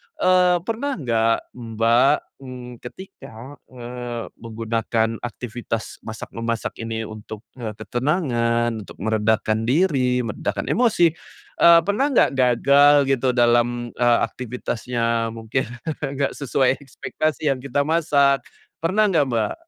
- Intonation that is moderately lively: Yes, average, 3.7 semitones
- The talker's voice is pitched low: Yes, low, 125 Hz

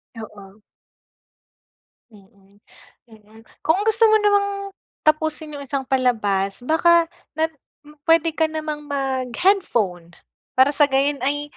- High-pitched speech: Yes, very high, 280 Hz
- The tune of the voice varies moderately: No, wide, 6.4 semitones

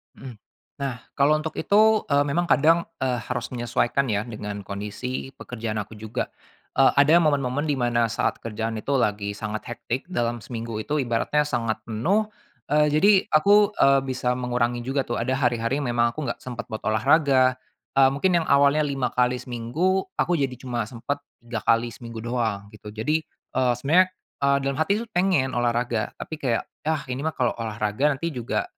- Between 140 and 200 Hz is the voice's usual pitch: No, low, 125 Hz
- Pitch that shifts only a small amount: No, average, 3.9 semitones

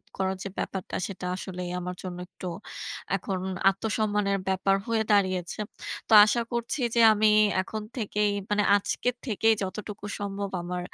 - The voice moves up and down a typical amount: No, narrow, 2.1 semitones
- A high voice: Yes, high, 200 Hz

